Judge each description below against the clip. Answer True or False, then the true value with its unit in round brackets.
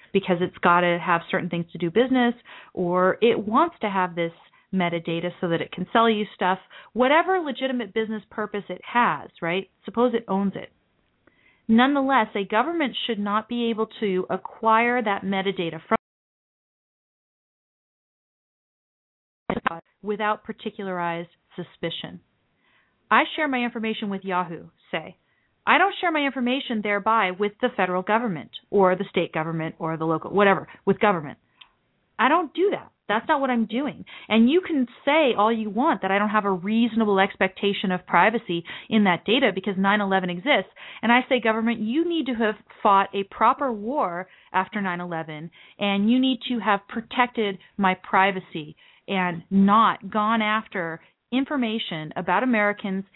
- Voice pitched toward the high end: True (210 Hz)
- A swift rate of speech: False (155 wpm)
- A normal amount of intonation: True (4.3 semitones)